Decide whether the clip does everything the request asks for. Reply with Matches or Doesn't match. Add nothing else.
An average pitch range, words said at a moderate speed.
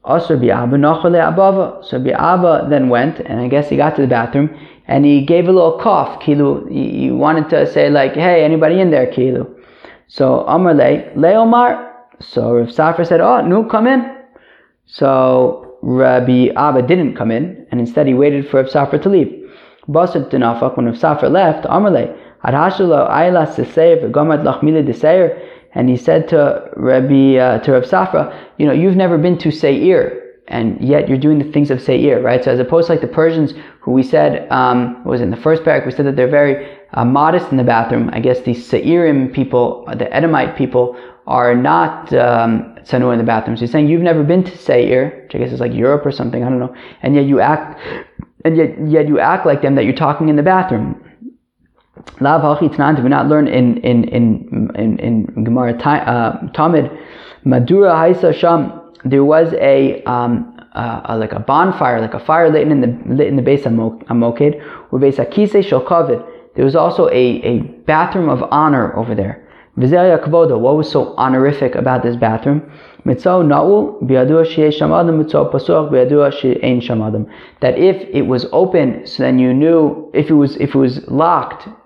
Matches